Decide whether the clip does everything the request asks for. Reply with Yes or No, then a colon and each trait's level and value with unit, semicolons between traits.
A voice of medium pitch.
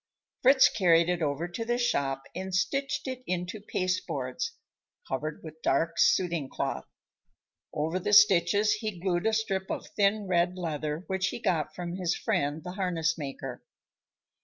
Yes: medium, 180 Hz